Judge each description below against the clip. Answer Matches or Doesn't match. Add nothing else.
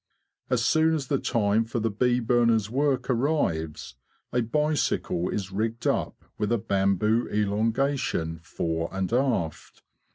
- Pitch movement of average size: Matches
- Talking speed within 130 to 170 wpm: Matches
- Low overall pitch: Matches